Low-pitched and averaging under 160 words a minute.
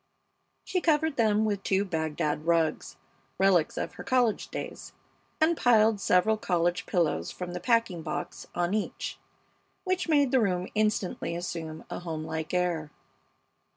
No: medium, 185 Hz; average, 140 wpm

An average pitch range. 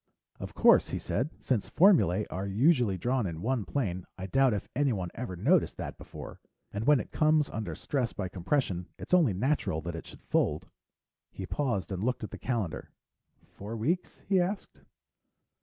No: wide, 7.0 semitones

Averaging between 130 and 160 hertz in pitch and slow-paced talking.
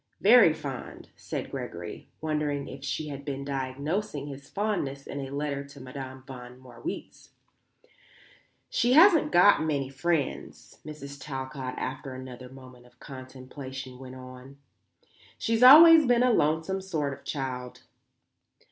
Yes: medium, 140 Hz; slow, 130 wpm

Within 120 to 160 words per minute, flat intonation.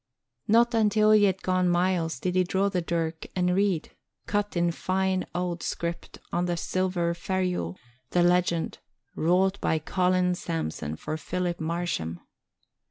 Yes: average, 145 wpm; narrow, 1.8 semitones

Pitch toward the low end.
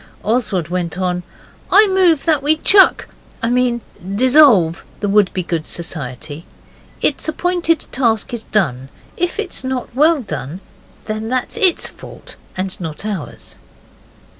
No: high, 225 Hz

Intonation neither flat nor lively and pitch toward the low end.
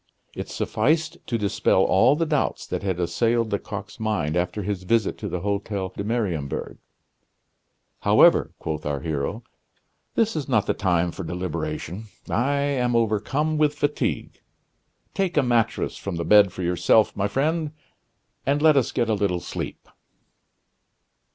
No: wide, 7.1 semitones; low, 105 Hz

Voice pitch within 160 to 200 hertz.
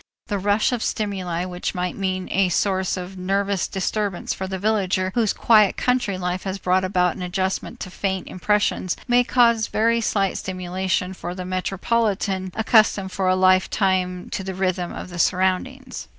Yes: high, 190 Hz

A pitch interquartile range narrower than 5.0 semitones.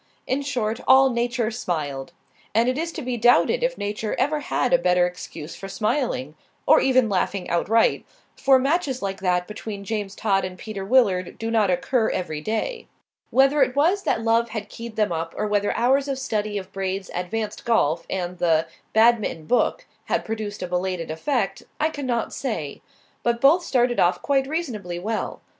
No: wide, 5.6 semitones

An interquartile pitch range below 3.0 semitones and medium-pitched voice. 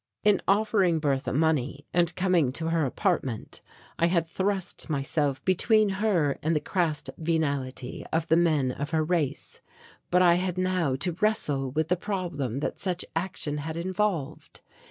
No: average, 4.1 semitones; medium, 165 Hz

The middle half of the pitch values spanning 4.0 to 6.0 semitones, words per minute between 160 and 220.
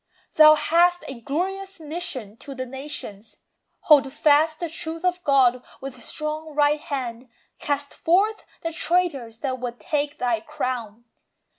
No: average, 4.3 semitones; average, 140 wpm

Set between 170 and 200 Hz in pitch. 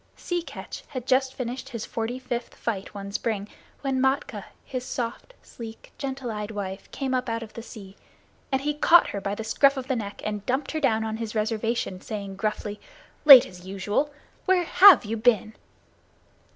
No: high, 230 Hz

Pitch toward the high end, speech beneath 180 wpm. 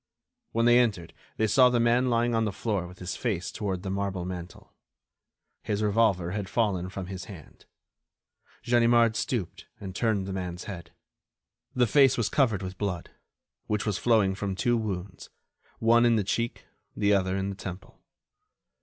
No: low, 100 Hz; average, 170 wpm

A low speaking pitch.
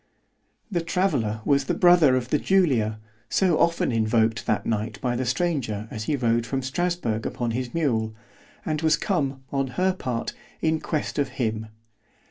Yes: low, 130 Hz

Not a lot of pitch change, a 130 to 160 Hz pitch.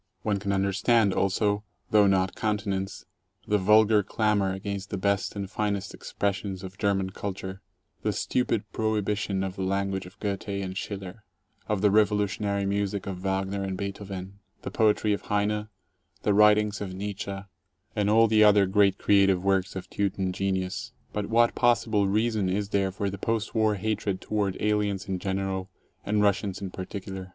No: narrow, 1.5 semitones; low, 100 Hz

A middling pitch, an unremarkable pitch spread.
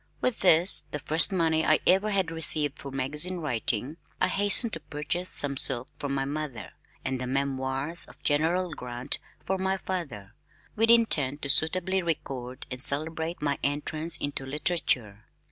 Yes: medium, 150 Hz; average, 4.3 semitones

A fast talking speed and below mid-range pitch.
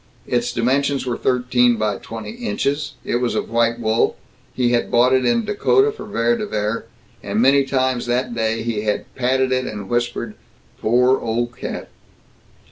No: average, 170 wpm; low, 120 Hz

